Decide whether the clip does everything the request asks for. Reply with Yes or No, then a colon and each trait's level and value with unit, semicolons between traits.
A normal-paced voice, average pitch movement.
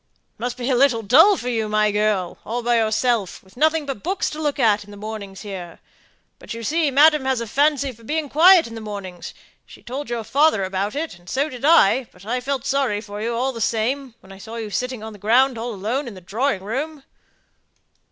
No: fast, 230 wpm; average, 4.7 semitones